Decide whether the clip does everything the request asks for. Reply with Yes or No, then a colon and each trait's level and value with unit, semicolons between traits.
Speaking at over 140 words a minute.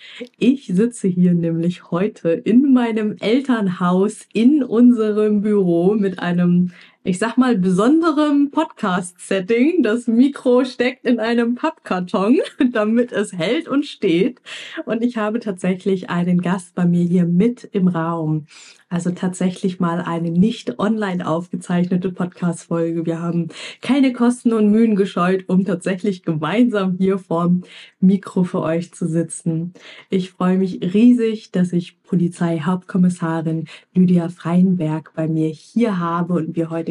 No: average, 135 wpm